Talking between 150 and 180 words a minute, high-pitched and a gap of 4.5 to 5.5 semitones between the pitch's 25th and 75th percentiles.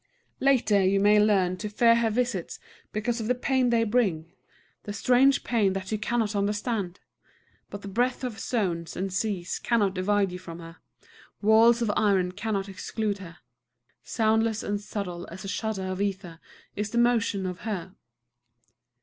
No: average, 165 wpm; high, 205 Hz; average, 3.3 semitones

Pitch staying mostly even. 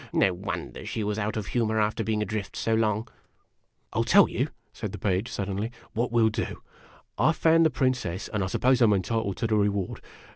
Yes: narrow, 2.3 semitones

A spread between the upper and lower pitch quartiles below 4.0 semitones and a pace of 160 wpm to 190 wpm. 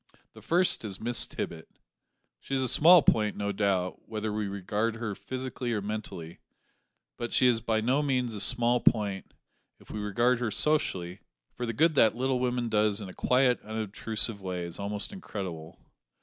Yes: average, 3.6 semitones; average, 180 wpm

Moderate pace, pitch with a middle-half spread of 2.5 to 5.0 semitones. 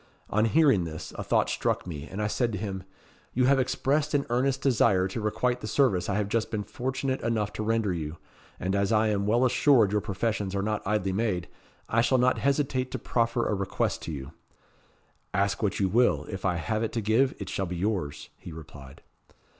No: fast, 210 wpm; average, 4.4 semitones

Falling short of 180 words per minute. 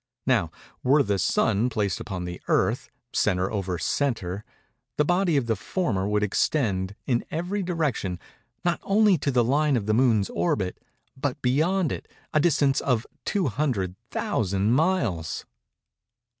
Yes: average, 140 wpm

